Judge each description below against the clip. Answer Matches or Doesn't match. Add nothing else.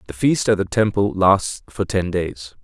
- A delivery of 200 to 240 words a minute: Matches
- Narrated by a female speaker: Doesn't match